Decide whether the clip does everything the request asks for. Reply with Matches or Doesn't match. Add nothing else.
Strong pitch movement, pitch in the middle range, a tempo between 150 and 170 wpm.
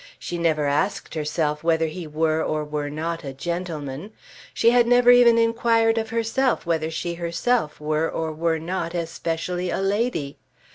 Matches